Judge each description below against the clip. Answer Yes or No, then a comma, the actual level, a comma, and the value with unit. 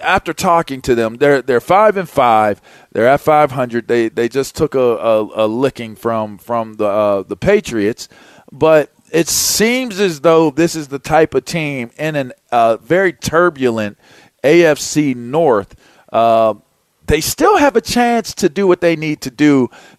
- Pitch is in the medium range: Yes, medium, 145 Hz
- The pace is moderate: Yes, average, 175 wpm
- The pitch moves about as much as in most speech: No, wide, 6.2 semitones